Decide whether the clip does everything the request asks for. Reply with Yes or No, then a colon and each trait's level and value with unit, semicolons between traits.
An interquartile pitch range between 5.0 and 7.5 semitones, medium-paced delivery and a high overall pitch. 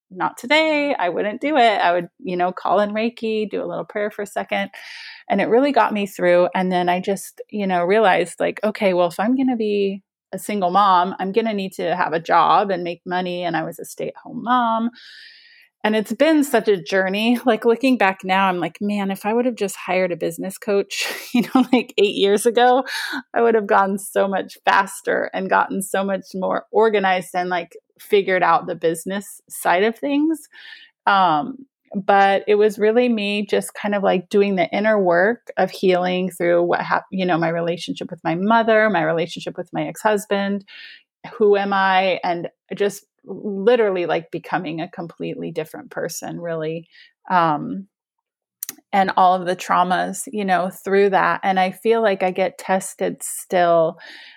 No: average, 4.2 semitones; average, 195 wpm; high, 200 Hz